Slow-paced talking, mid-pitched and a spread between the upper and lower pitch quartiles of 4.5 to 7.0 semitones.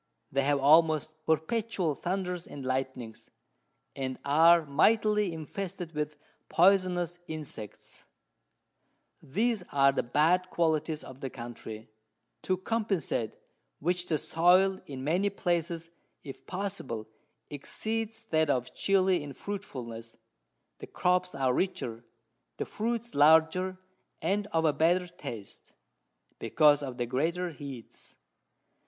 Yes: slow, 115 wpm; medium, 160 Hz; average, 5.0 semitones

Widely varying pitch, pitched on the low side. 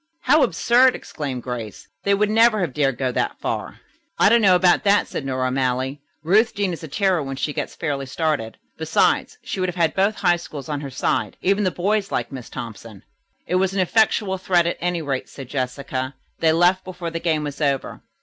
No: wide, 5.9 semitones; medium, 165 Hz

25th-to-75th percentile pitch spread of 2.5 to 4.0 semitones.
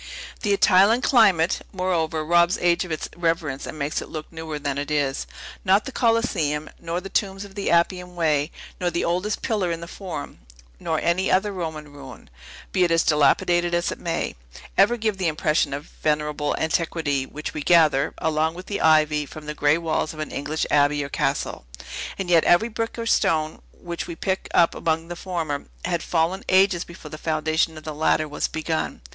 Yes: average, 3.1 semitones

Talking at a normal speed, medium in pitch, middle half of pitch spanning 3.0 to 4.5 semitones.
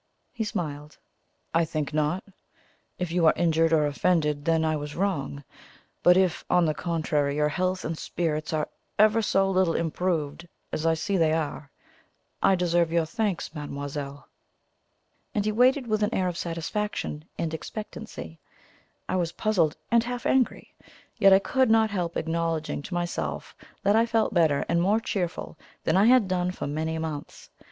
Yes: average, 165 wpm; medium, 170 Hz; average, 3.9 semitones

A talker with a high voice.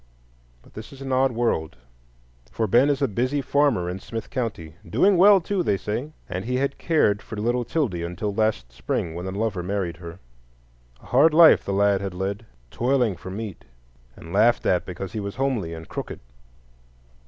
No: low, 110 Hz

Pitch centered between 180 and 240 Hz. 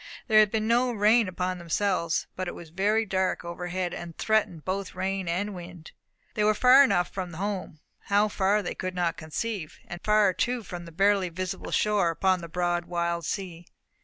Yes: medium, 185 Hz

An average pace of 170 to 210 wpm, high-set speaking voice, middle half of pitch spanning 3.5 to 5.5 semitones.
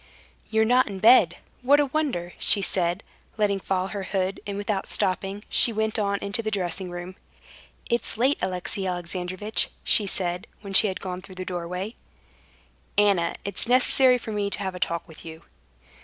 No: average, 175 wpm; high, 195 Hz; average, 3.0 semitones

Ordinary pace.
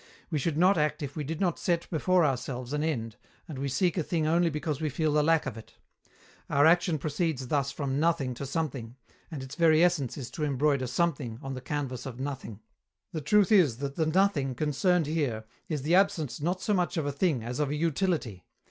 No: fast, 220 wpm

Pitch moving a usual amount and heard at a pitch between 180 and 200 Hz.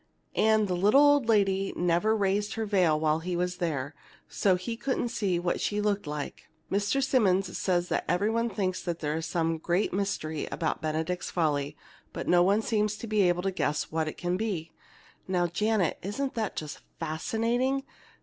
Yes: average, 4.3 semitones; medium, 185 Hz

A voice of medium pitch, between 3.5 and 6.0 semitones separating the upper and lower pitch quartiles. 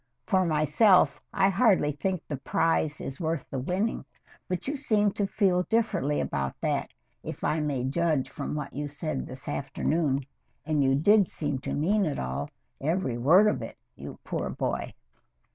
Yes: medium, 155 Hz; wide, 5.5 semitones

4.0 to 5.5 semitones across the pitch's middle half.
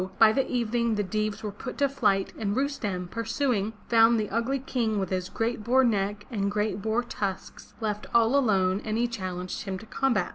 No: average, 3.0 semitones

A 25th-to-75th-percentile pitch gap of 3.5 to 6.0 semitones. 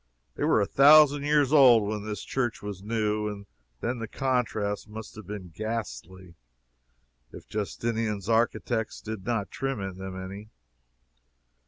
No: average, 2.9 semitones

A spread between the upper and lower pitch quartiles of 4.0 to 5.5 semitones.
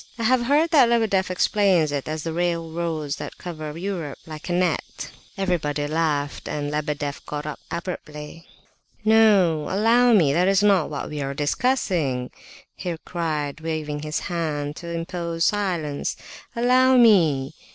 Yes: average, 4.7 semitones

